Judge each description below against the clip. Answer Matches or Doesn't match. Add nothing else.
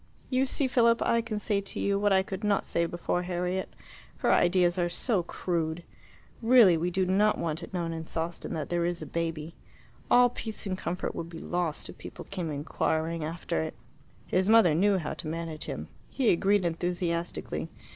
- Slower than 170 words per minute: Doesn't match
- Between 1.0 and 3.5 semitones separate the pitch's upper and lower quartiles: Matches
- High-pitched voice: Doesn't match